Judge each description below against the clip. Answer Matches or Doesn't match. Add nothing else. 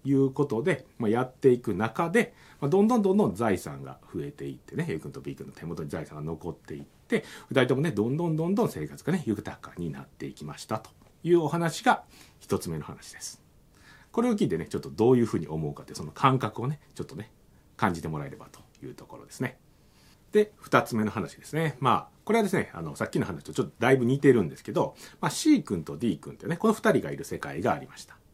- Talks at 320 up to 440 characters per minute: Matches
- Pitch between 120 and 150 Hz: Matches